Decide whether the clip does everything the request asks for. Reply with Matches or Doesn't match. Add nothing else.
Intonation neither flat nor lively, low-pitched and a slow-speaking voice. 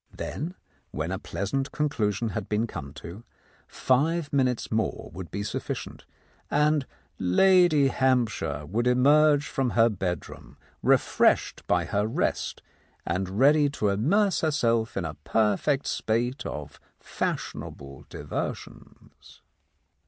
Doesn't match